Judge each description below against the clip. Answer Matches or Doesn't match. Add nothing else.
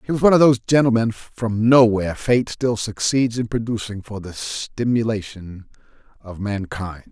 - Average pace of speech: Matches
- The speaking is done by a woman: Doesn't match